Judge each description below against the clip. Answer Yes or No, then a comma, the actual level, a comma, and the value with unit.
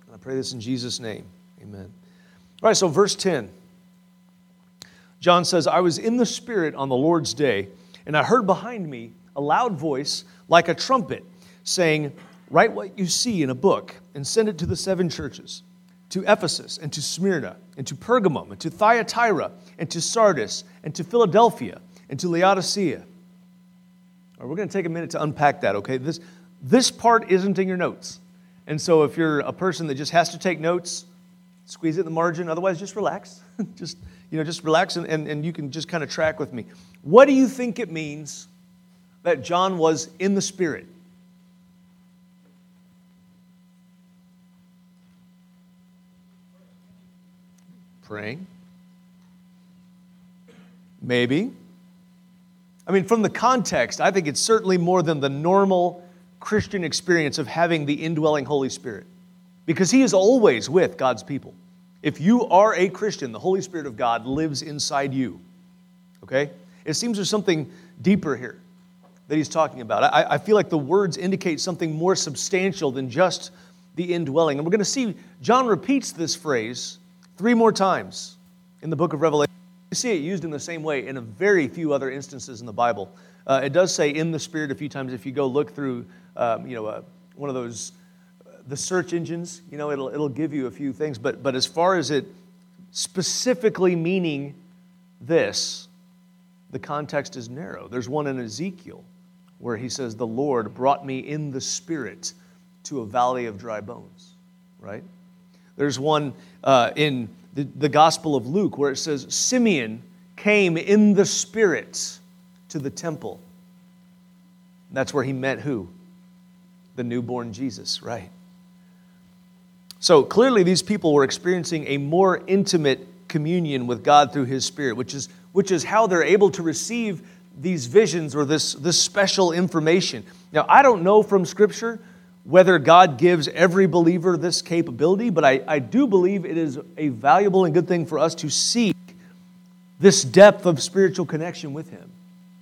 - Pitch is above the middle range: No, medium, 180 Hz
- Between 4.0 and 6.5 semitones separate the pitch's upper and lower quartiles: No, average, 3.2 semitones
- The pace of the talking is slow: No, average, 170 wpm